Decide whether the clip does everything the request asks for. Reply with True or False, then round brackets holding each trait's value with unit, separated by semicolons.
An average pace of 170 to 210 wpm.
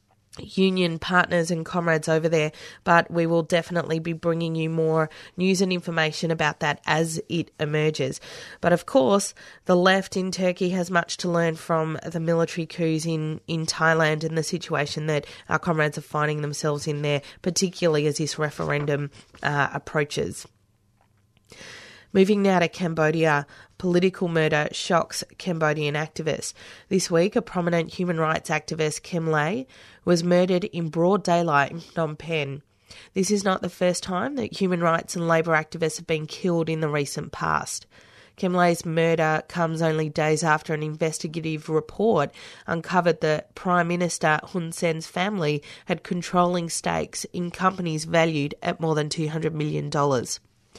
False (155 wpm)